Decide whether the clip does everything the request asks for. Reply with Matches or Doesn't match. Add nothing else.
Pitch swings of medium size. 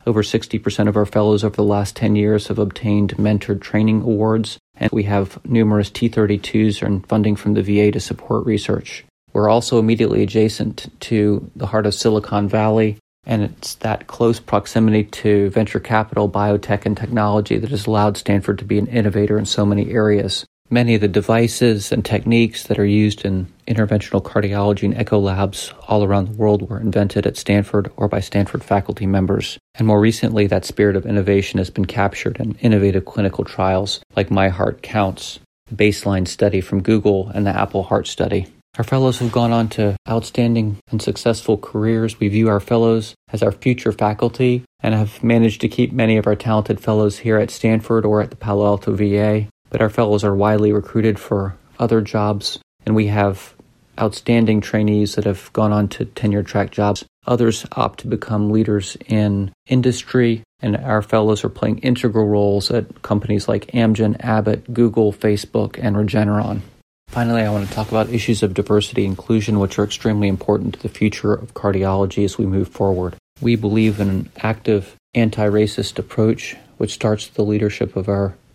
Doesn't match